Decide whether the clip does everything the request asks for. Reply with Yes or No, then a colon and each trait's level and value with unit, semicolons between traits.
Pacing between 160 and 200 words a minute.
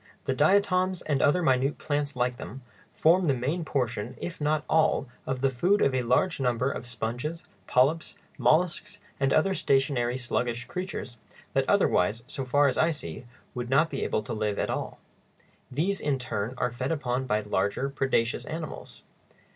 Yes: average, 170 wpm